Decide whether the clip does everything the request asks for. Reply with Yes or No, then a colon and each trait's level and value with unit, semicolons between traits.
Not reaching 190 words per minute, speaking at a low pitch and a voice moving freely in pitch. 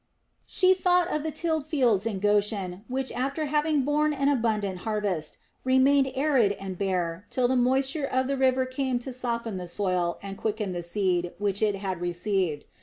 No: average, 180 wpm; high, 230 Hz; wide, 6.0 semitones